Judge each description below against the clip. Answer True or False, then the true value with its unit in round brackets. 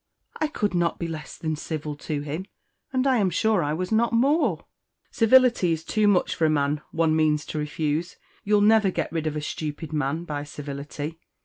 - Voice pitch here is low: False (160 Hz)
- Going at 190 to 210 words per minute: True (200 wpm)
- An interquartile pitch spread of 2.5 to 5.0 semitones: False (5.6 semitones)